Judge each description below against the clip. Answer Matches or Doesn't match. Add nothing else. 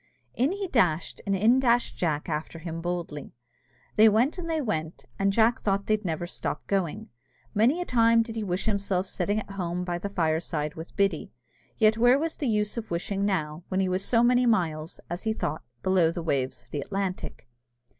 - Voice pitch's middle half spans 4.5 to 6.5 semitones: Matches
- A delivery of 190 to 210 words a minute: Matches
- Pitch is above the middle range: Matches